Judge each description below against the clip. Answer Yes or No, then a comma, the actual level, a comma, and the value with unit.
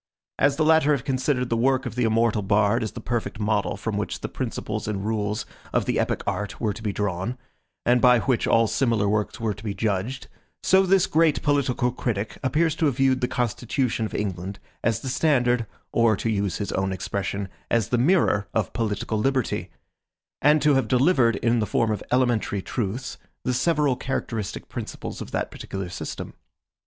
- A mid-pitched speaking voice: No, low, 115 Hz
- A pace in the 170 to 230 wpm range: Yes, average, 190 wpm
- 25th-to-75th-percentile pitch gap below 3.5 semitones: No, average, 3.9 semitones